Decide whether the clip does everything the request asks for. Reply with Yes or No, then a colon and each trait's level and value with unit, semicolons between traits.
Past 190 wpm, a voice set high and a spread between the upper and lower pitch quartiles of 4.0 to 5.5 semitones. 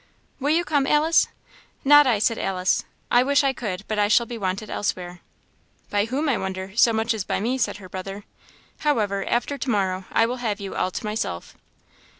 Yes: average, 200 wpm; high, 220 Hz; average, 4.9 semitones